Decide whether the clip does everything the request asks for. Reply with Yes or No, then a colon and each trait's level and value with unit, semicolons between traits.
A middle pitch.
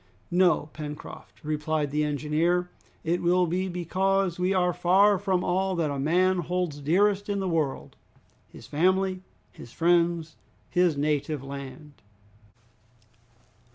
Yes: medium, 175 Hz